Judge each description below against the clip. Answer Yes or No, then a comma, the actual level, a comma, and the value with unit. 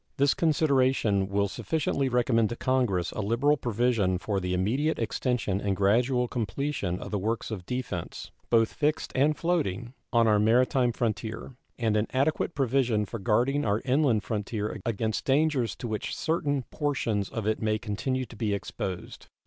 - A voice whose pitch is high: No, low, 115 Hz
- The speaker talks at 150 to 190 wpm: Yes, average, 160 wpm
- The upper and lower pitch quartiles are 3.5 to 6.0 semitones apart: Yes, average, 4.2 semitones